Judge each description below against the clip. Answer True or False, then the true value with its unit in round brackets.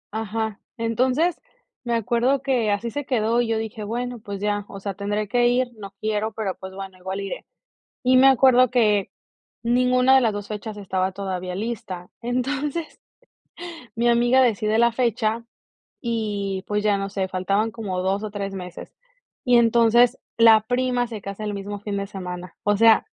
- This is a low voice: False (220 Hz)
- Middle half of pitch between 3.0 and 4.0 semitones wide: True (3.3 semitones)